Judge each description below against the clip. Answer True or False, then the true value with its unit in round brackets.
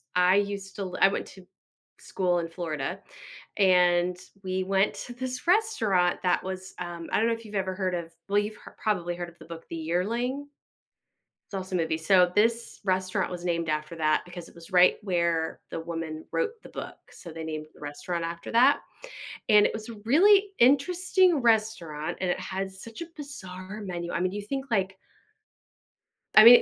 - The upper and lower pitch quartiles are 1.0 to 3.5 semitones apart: False (4.1 semitones)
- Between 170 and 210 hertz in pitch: True (185 Hz)